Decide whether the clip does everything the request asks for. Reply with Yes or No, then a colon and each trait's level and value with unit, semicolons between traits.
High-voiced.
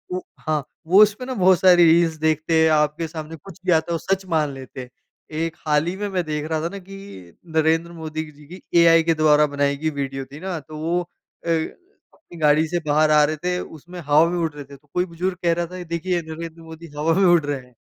No: medium, 160 Hz